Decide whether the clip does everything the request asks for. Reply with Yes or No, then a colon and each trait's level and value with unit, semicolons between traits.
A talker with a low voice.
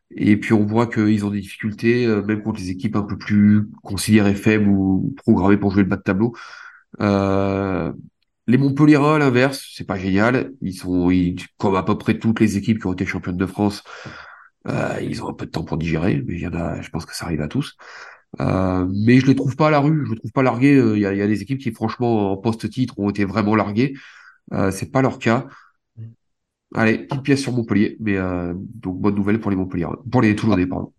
Yes: low, 105 Hz